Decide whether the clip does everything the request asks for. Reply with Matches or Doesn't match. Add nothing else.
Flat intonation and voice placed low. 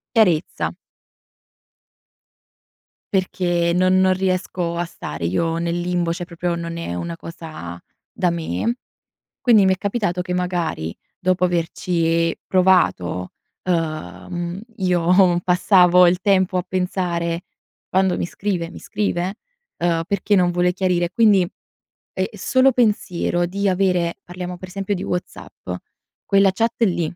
Doesn't match